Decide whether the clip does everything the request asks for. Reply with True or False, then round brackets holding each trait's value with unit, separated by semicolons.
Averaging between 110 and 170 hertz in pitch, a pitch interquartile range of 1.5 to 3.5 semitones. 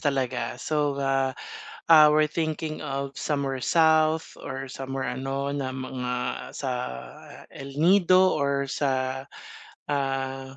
True (135 Hz; 2.4 semitones)